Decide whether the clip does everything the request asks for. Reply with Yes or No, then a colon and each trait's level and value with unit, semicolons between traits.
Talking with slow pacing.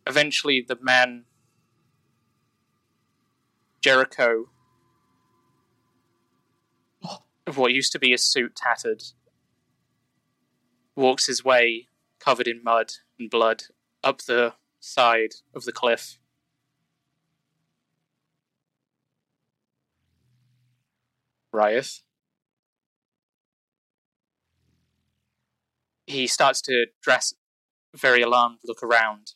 Yes: slow, 75 wpm